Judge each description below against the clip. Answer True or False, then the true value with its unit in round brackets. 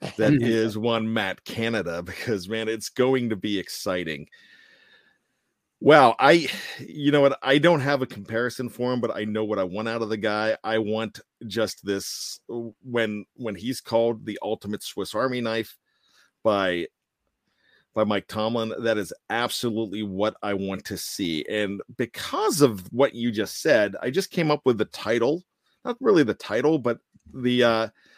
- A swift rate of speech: False (170 wpm)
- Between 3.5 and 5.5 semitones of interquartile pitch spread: False (3.0 semitones)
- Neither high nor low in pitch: False (115 Hz)